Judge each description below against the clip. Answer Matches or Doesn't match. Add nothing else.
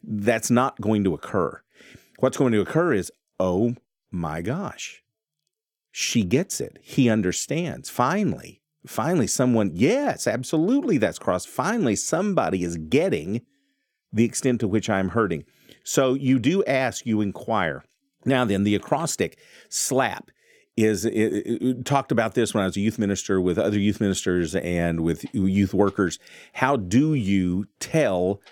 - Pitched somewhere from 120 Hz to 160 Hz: Doesn't match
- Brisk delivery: Doesn't match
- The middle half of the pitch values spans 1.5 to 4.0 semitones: Doesn't match